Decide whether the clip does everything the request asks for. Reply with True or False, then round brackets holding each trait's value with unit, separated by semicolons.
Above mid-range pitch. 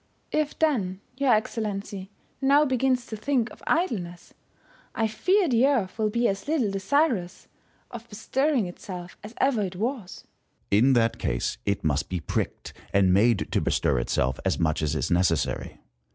True (210 Hz)